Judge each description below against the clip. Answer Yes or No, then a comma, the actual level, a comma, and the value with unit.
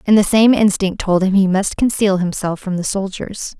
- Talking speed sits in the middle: No, fast, 215 wpm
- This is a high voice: Yes, high, 195 Hz